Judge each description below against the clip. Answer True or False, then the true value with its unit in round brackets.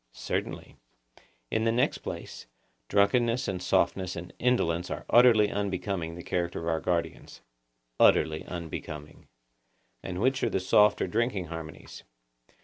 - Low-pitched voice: True (95 Hz)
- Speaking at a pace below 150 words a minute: True (135 wpm)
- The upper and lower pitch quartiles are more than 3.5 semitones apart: True (4.7 semitones)